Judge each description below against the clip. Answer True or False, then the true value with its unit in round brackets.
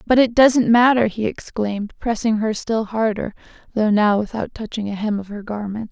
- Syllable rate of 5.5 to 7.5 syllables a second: False (5.0 syllables/s)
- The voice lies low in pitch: False (220 Hz)